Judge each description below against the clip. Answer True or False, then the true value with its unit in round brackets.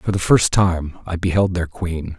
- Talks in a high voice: False (90 Hz)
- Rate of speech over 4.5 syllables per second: False (4.3 syllables/s)